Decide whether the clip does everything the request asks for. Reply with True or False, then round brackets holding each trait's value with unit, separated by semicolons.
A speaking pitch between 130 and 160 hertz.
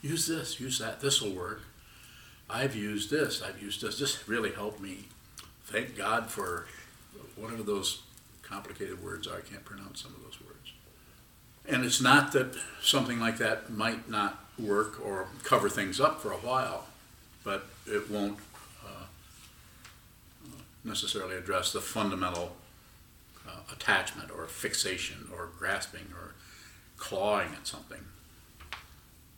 False (105 Hz)